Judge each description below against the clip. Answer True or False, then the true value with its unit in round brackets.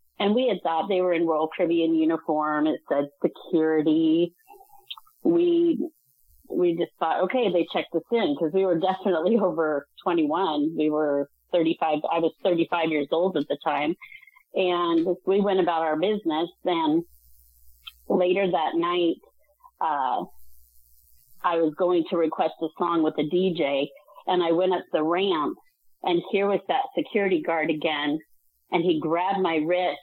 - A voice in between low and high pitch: True (175 Hz)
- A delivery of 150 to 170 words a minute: True (155 wpm)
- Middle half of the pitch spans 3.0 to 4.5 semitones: True (4.2 semitones)